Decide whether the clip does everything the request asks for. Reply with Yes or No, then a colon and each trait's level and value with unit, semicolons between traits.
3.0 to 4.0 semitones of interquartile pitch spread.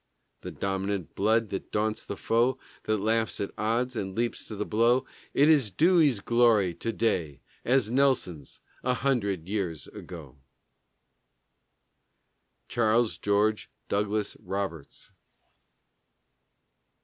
Yes: average, 3.4 semitones